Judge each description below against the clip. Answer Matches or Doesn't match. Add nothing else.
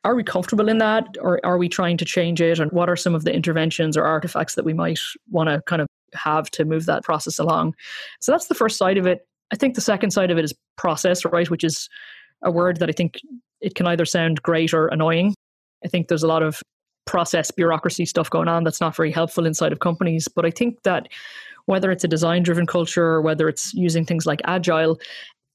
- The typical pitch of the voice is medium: Matches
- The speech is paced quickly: Matches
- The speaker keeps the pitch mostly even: Matches